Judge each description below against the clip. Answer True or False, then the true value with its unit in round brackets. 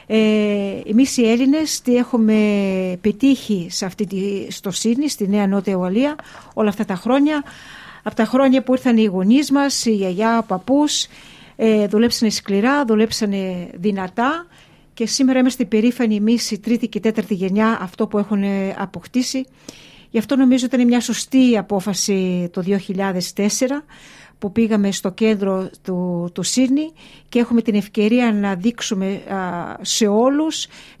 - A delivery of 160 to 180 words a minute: False (145 wpm)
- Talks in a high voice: True (220 Hz)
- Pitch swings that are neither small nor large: True (3.8 semitones)